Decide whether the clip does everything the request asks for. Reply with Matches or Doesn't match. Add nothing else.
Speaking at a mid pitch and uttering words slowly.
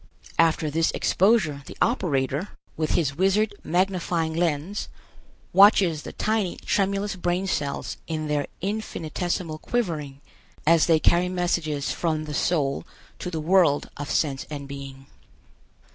Matches